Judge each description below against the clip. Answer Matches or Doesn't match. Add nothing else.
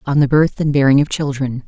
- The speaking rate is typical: Doesn't match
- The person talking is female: Matches